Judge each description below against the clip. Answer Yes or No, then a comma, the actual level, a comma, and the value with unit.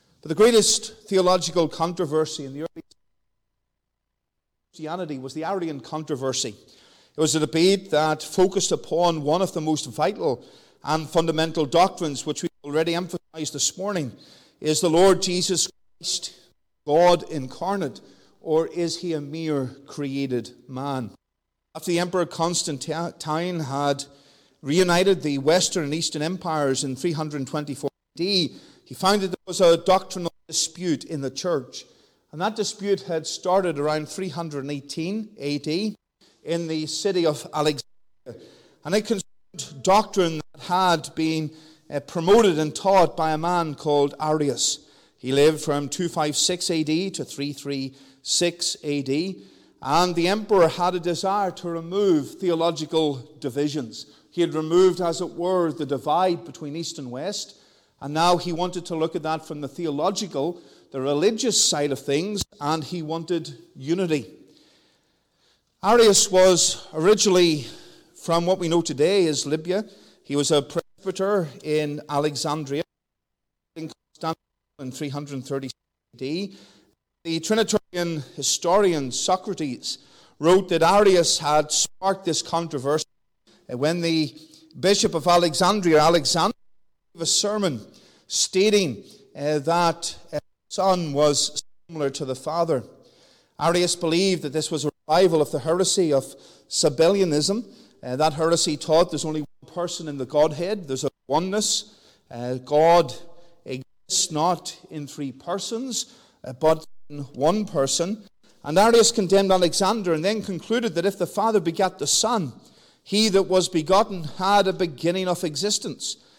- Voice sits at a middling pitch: Yes, medium, 165 Hz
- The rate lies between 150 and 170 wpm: No, slow, 135 wpm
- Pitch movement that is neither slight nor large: Yes, average, 3.6 semitones